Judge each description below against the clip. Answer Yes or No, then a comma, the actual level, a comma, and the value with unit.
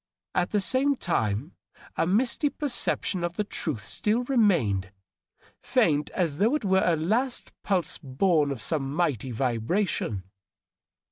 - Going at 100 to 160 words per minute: Yes, slow, 135 wpm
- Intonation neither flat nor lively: No, wide, 7.5 semitones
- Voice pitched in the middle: Yes, medium, 175 Hz